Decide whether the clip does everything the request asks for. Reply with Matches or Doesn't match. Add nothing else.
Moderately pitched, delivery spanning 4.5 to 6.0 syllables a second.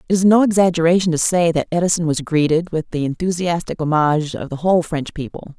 Doesn't match